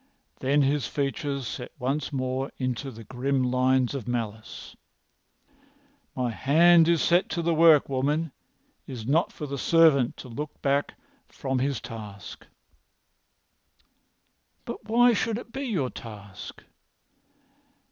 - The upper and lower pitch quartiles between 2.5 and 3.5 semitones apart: No, average, 3.9 semitones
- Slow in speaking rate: Yes, slow, 130 wpm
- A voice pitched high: No, low, 135 Hz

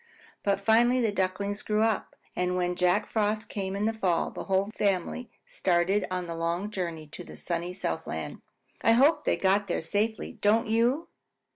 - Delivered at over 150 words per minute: Yes, average, 175 wpm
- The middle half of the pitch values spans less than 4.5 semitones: Yes, average, 3.3 semitones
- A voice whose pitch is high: Yes, high, 200 Hz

